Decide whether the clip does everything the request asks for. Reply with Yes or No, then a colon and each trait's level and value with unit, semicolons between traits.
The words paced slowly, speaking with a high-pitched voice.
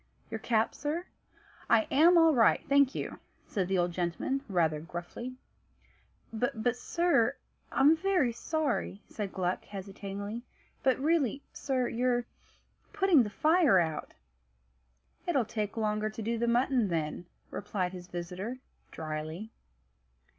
Yes: slow, 125 wpm; high, 225 Hz